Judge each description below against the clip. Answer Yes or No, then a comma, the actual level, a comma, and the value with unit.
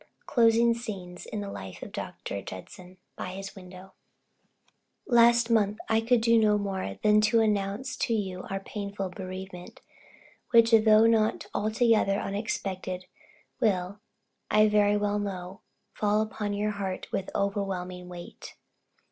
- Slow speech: Yes, slow, 130 wpm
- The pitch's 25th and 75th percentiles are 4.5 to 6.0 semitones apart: No, average, 2.8 semitones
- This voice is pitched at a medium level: No, high, 205 Hz